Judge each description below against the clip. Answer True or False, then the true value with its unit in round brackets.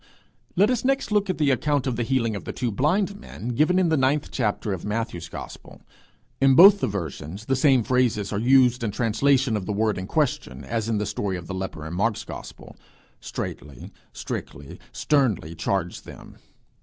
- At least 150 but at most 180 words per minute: False (195 wpm)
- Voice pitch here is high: False (115 Hz)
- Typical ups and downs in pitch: False (6.1 semitones)